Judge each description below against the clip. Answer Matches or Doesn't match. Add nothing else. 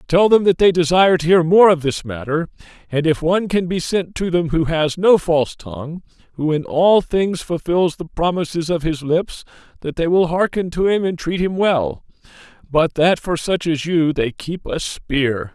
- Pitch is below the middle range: Doesn't match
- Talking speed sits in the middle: Doesn't match